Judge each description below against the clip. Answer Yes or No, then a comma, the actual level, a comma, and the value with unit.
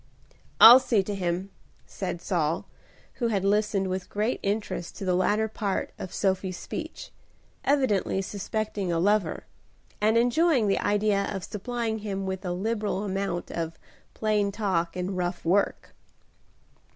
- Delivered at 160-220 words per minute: No, average, 140 wpm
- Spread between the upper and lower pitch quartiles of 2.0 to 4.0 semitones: Yes, narrow, 2.5 semitones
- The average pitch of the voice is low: No, high, 200 Hz